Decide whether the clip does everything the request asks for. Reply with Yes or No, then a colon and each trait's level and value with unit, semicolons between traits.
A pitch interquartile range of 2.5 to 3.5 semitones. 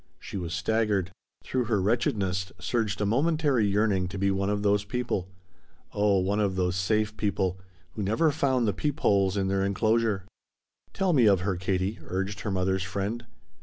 Yes: average, 2.8 semitones